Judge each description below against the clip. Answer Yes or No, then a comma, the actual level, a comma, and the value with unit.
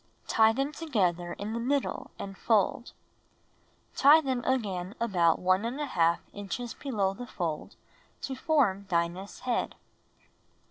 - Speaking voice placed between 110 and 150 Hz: No, high, 215 Hz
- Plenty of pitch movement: Yes, wide, 5.8 semitones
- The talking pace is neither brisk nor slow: No, slow, 125 wpm